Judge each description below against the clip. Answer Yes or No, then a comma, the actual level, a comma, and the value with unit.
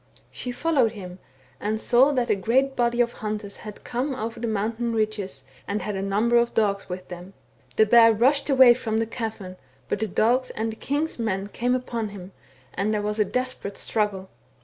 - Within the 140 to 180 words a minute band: No, average, 195 wpm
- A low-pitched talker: No, high, 220 Hz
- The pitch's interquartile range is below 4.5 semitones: Yes, average, 3.0 semitones